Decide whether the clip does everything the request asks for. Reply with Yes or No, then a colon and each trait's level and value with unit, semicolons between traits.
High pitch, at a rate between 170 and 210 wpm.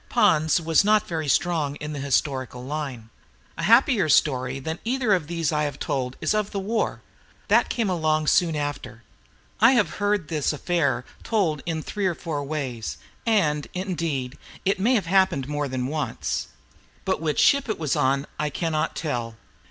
No: medium, 155 Hz; average, 175 wpm